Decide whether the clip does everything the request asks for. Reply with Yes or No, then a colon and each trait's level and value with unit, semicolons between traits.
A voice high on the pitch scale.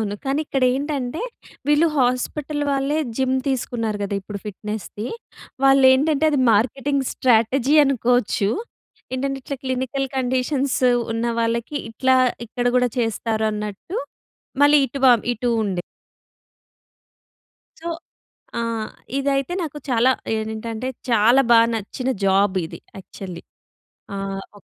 Yes: very high, 250 Hz